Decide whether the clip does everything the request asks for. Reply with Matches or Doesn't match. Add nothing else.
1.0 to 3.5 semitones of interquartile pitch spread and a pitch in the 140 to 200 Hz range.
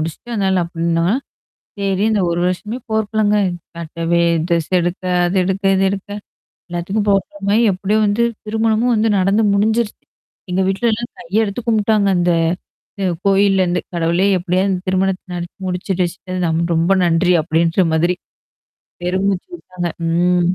Matches